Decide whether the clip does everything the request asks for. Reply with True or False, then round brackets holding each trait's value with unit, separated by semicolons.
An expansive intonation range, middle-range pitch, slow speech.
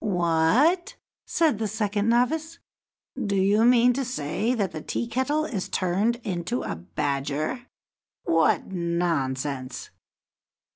False (7.2 semitones; 205 Hz; 115 wpm)